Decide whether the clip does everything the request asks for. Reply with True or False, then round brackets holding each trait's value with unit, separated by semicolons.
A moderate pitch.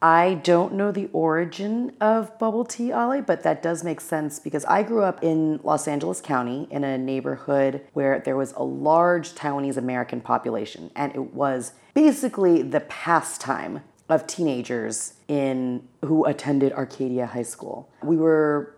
True (150 Hz)